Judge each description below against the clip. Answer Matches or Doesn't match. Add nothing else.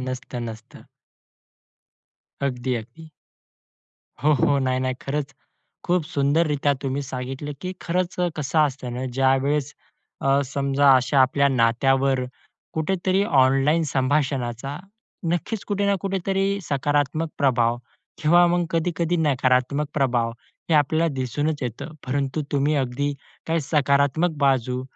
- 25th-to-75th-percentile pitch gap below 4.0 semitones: Matches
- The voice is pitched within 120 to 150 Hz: Matches